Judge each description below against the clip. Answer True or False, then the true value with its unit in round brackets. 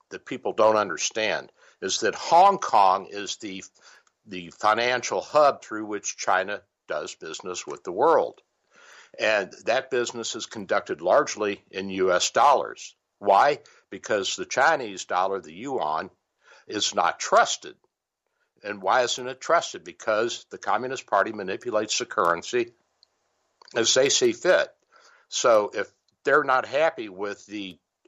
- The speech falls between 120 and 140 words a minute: True (135 wpm)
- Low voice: True (125 Hz)